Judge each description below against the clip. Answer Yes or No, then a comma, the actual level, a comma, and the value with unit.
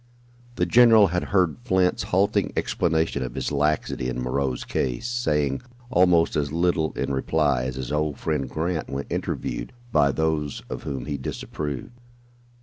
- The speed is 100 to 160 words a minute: Yes, average, 150 wpm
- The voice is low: Yes, very low, 75 Hz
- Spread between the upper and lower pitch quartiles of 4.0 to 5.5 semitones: Yes, average, 4.5 semitones